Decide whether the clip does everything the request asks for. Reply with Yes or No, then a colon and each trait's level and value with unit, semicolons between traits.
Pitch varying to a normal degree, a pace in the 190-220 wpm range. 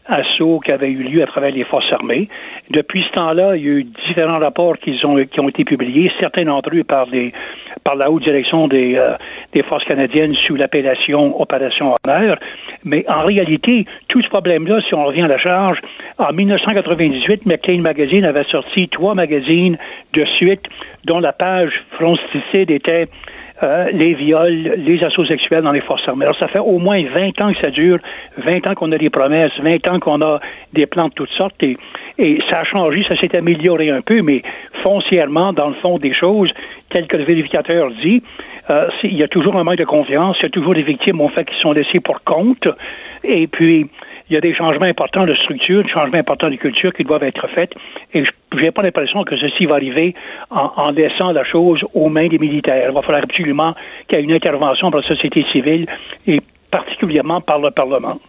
Yes: average, 3.6 semitones; average, 210 wpm